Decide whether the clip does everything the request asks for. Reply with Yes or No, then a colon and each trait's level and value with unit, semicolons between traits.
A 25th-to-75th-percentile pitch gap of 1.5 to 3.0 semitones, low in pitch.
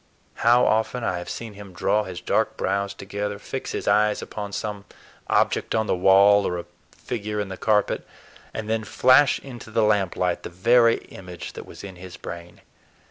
Yes: average, 2.7 semitones; low, 105 Hz